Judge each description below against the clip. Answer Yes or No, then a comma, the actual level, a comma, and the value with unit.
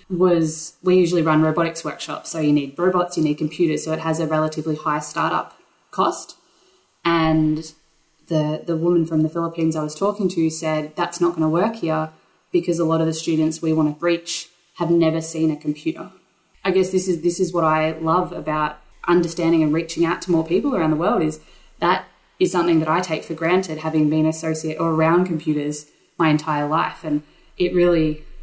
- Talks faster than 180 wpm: Yes, average, 200 wpm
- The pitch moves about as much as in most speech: No, narrow, 1.7 semitones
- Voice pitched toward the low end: No, medium, 160 Hz